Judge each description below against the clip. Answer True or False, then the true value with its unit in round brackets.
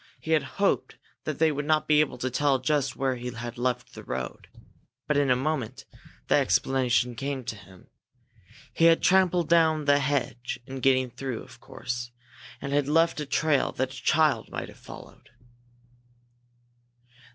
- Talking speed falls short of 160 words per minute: False (170 wpm)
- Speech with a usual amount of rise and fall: True (3.5 semitones)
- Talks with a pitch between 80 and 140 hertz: True (135 Hz)